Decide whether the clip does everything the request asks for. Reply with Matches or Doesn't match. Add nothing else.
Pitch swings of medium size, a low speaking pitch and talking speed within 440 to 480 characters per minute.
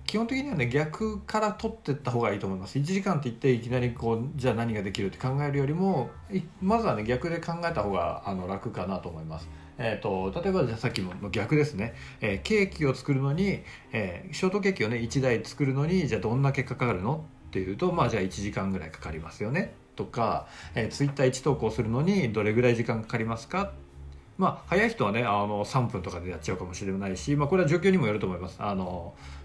Doesn't match